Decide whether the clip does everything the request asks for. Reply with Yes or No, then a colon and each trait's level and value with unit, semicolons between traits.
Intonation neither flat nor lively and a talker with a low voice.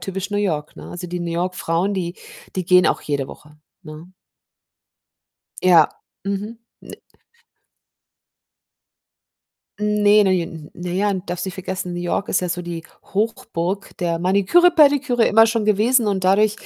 No: average, 3.1 semitones; medium, 185 Hz